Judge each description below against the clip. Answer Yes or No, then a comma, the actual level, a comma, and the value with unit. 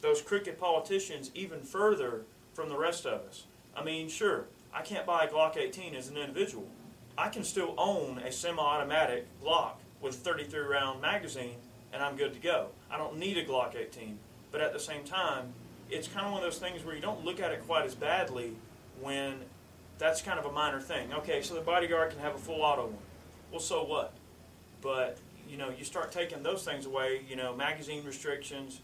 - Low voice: No, medium, 145 Hz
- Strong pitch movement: No, average, 4.6 semitones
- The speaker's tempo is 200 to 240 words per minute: Yes, fast, 205 wpm